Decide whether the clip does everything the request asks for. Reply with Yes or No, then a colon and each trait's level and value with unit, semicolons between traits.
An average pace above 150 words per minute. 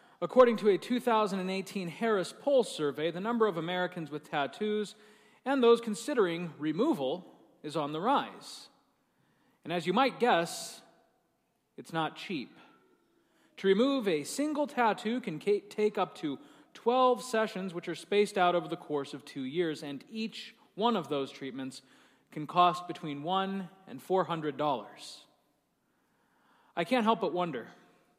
No: average, 145 wpm